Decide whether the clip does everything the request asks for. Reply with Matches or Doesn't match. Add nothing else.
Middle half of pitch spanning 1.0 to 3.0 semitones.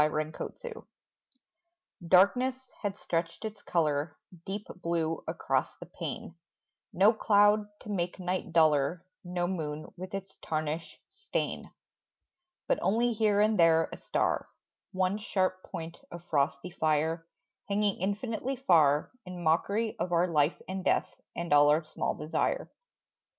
Doesn't match